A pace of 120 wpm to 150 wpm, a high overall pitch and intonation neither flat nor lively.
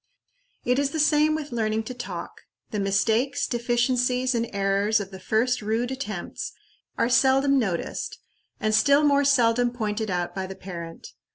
No: average, 160 wpm; high, 235 Hz; average, 4.0 semitones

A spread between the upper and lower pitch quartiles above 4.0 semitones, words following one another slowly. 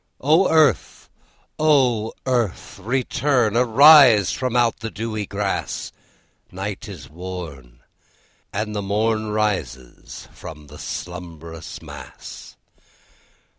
Yes: wide, 5.4 semitones; slow, 95 wpm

